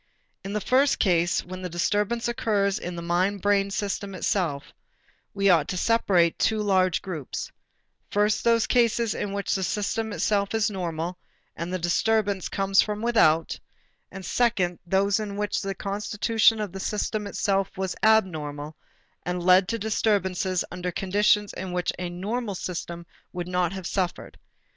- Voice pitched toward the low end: No, high, 195 Hz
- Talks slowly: No, average, 160 wpm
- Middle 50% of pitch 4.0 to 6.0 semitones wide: No, average, 2.8 semitones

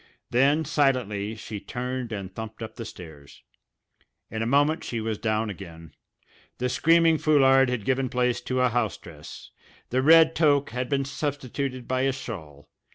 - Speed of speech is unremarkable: Yes, average, 160 wpm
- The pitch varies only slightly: No, average, 4.1 semitones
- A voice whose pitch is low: Yes, low, 125 Hz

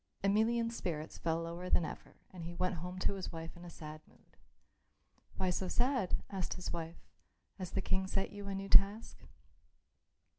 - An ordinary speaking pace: Yes, average, 180 wpm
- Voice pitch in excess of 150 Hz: Yes, medium, 185 Hz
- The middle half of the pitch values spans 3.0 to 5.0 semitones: No, narrow, 2.6 semitones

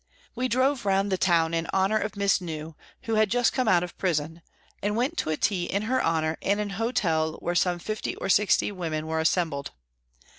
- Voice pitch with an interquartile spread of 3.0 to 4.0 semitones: No, average, 4.8 semitones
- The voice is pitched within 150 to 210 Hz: Yes, high, 190 Hz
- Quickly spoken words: Yes, fast, 210 wpm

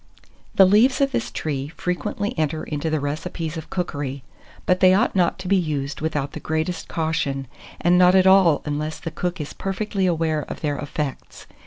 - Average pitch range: Yes, average, 3.8 semitones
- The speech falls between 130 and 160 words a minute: No, average, 185 wpm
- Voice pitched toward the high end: No, medium, 165 Hz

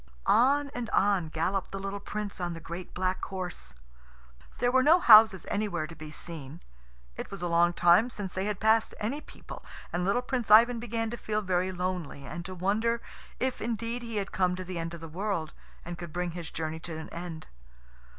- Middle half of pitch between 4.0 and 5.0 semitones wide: Yes, average, 4.3 semitones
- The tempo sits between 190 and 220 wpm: Yes, fast, 205 wpm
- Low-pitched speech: No, high, 190 Hz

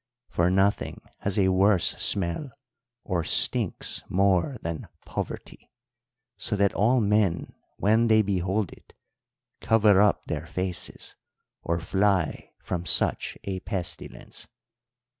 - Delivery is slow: Yes, slow, 115 wpm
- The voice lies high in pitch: No, very low, 95 Hz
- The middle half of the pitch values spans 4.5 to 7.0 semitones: No, narrow, 2.5 semitones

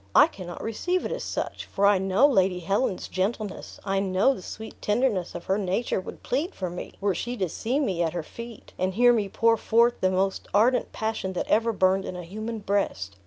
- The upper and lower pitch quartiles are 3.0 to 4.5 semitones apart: Yes, average, 3.7 semitones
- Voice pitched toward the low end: No, high, 200 Hz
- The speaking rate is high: Yes, fast, 215 wpm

